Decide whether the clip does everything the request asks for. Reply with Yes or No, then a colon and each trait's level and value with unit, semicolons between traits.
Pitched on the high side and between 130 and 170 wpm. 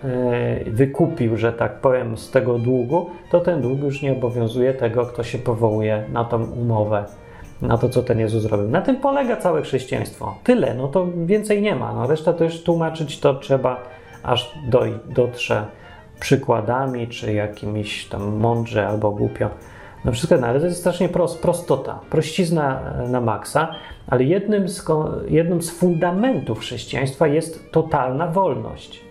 No: low, 130 Hz; average, 155 wpm